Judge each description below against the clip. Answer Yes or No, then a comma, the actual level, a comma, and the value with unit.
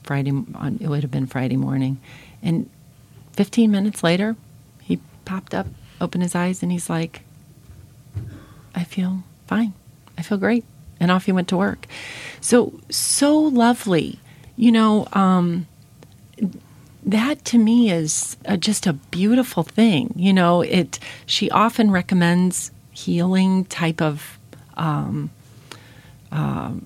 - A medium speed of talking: No, slow, 130 wpm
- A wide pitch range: Yes, wide, 6.9 semitones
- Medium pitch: Yes, medium, 170 Hz